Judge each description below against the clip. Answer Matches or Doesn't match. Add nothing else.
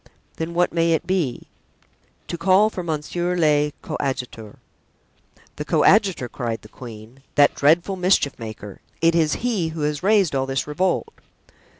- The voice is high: Doesn't match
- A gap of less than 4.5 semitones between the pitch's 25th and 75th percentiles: Doesn't match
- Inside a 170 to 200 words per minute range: Doesn't match